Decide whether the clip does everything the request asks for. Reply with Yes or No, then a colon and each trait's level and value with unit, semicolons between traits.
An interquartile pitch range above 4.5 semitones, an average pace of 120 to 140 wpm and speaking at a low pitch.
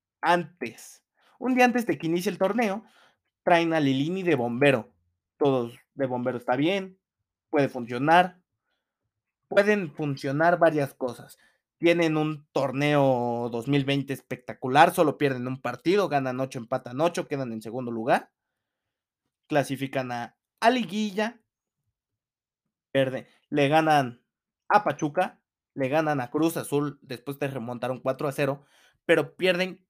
No: average, 4.9 semitones; slow, 125 wpm; medium, 145 Hz